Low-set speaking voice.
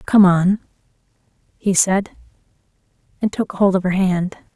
No: high, 190 Hz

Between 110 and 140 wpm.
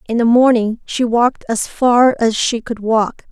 No: average, 200 wpm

